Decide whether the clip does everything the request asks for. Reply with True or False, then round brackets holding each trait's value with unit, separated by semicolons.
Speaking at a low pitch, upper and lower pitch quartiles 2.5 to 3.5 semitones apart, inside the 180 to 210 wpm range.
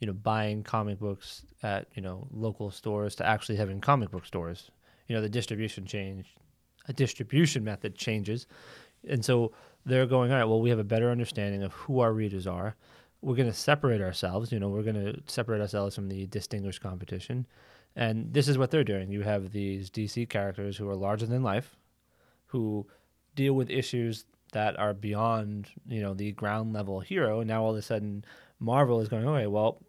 True (110 Hz; 3.1 semitones; 200 wpm)